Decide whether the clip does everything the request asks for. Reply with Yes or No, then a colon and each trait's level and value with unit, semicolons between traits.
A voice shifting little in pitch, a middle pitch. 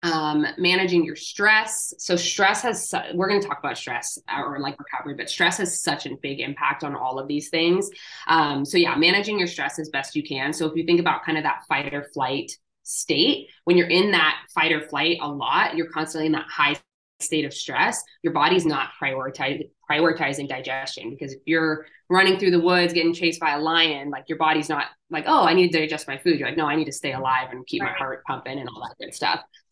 No: average, 3.2 semitones; medium, 160 Hz